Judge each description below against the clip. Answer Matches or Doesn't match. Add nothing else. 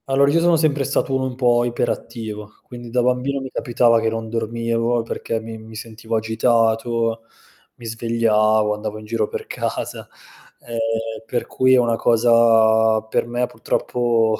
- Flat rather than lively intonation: Matches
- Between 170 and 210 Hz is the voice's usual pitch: Doesn't match